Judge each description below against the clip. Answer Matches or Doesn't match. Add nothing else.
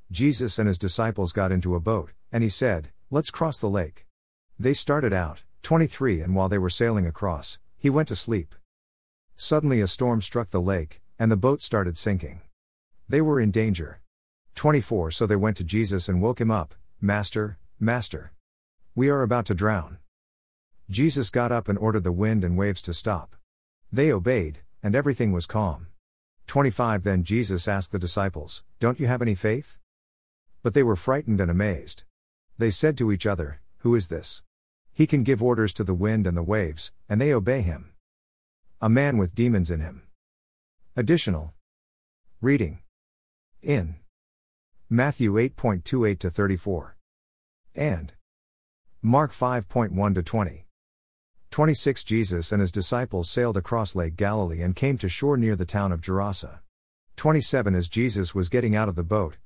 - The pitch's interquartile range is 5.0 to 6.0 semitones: Matches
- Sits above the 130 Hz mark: Doesn't match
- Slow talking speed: Doesn't match